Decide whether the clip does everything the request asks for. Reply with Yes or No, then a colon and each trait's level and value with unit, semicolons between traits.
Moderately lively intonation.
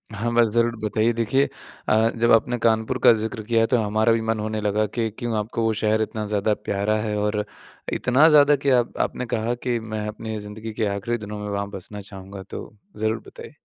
No: narrow, 1.9 semitones